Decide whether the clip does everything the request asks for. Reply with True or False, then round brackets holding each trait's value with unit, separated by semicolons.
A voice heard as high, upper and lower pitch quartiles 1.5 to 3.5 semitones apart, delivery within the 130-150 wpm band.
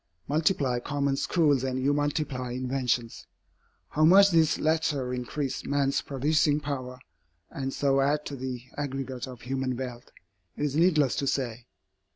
False (135 Hz; 2.5 semitones; 145 wpm)